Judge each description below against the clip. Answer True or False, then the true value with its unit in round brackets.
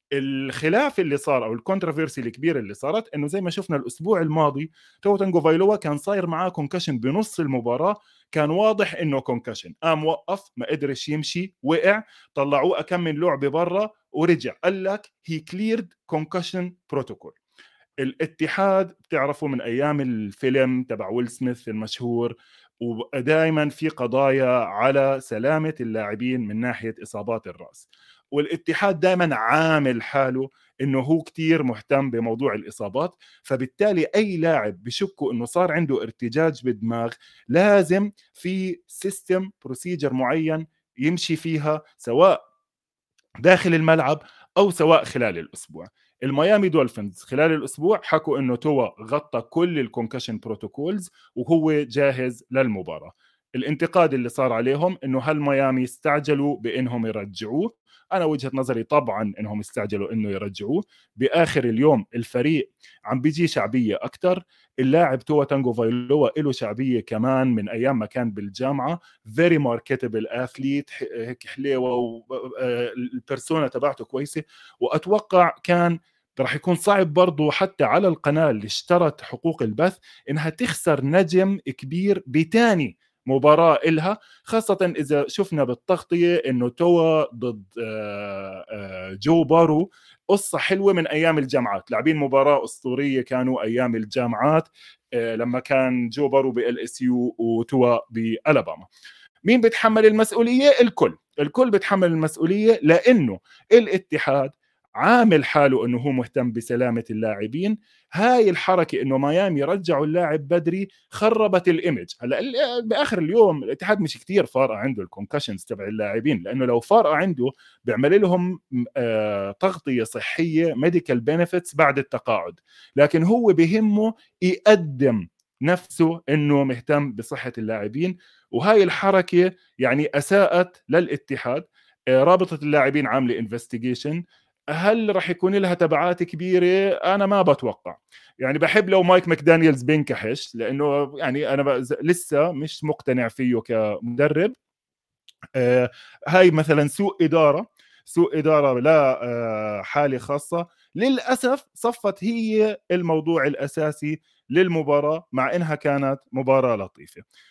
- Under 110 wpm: False (120 wpm)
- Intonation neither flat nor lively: False (5.8 semitones)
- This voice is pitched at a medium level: True (150 Hz)